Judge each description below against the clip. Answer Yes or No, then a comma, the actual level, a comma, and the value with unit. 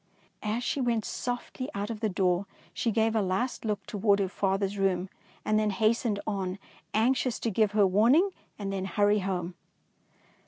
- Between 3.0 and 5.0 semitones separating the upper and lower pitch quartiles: No, narrow, 2.6 semitones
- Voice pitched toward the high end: Yes, high, 210 Hz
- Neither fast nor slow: Yes, average, 170 wpm